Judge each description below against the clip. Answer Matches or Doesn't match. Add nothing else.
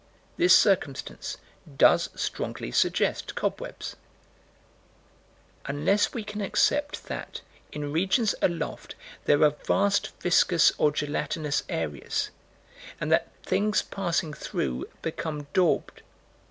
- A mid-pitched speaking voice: Matches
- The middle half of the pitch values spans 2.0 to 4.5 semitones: Doesn't match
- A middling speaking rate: Doesn't match